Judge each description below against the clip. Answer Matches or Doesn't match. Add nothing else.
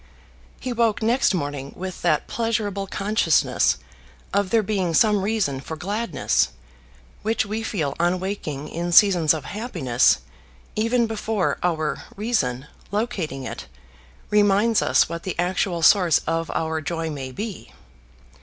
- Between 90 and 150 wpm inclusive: Matches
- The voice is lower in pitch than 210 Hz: Matches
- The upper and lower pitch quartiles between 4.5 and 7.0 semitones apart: Matches